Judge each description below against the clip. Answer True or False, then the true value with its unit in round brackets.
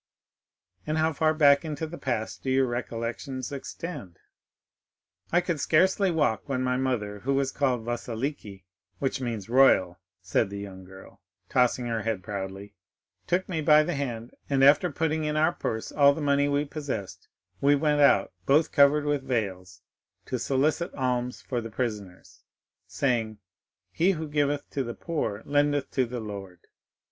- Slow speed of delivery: False (160 wpm)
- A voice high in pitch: False (130 Hz)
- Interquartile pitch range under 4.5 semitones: False (4.8 semitones)